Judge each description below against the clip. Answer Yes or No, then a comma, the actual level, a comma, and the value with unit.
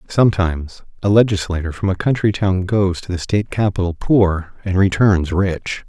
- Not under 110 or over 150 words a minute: No, average, 165 wpm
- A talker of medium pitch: No, very low, 95 Hz